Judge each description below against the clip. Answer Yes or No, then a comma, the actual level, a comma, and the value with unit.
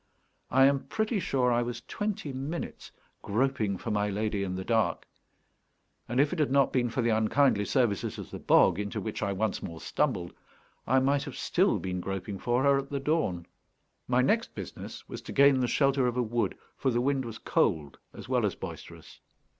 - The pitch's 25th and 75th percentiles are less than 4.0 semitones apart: No, average, 5.0 semitones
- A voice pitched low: Yes, low, 125 Hz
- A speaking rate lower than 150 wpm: No, average, 200 wpm